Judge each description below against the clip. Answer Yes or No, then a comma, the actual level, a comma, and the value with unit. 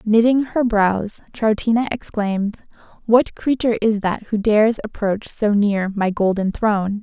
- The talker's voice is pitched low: No, high, 215 Hz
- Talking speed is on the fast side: No, average, 145 wpm